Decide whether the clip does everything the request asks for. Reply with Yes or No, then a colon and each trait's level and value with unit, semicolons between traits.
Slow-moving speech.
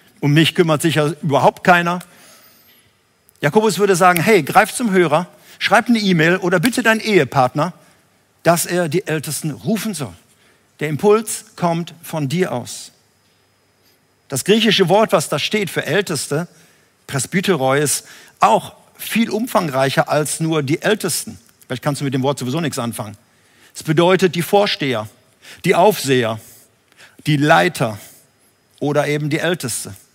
No: average, 140 wpm